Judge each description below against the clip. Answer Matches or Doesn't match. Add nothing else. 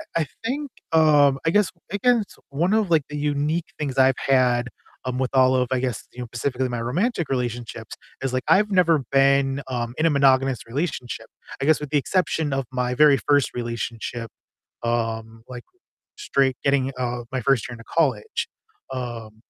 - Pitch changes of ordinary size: Matches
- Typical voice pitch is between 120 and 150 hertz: Matches